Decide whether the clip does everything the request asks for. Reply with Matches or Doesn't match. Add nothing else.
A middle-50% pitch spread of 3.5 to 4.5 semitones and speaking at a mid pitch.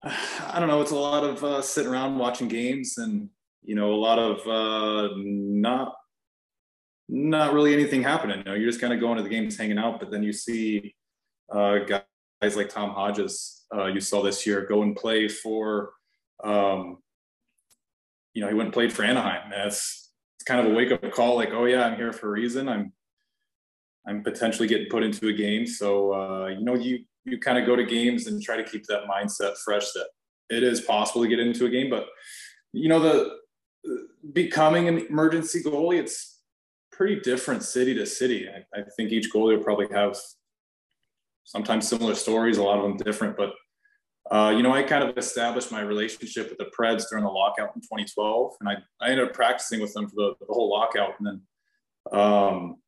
Doesn't match